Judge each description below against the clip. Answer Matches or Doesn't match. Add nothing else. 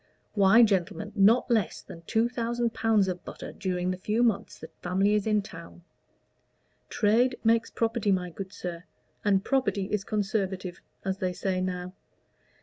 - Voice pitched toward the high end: Matches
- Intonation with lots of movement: Doesn't match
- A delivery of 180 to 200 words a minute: Doesn't match